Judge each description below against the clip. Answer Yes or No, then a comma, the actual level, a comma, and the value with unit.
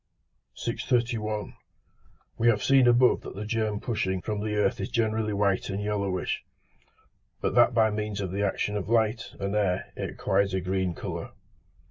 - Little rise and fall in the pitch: Yes, narrow, 2.3 semitones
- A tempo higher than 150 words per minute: Yes, average, 165 wpm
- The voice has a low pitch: Yes, low, 105 Hz